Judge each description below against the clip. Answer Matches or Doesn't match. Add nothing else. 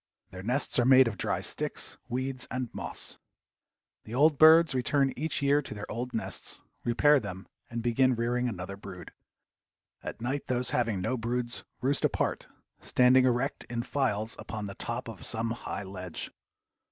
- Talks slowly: Doesn't match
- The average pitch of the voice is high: Doesn't match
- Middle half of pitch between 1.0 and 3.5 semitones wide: Matches